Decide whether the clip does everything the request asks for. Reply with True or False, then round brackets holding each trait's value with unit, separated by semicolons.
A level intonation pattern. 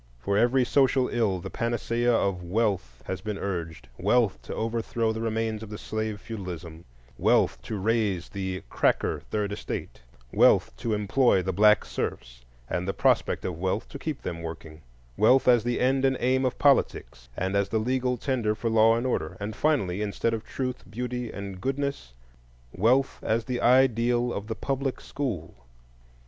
False (4.5 semitones)